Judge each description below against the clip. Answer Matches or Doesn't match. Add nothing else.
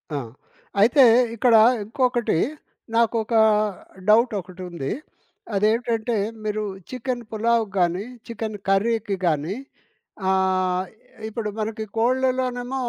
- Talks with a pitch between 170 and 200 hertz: Doesn't match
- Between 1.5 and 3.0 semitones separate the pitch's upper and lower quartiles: Doesn't match